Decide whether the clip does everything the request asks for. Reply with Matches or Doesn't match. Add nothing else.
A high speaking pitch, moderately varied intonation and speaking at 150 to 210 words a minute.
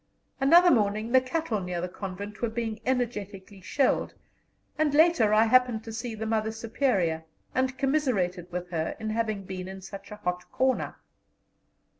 Matches